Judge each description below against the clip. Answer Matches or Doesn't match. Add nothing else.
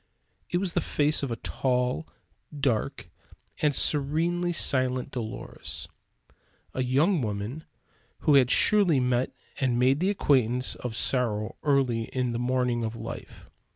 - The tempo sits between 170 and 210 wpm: Doesn't match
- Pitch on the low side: Matches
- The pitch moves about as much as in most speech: Matches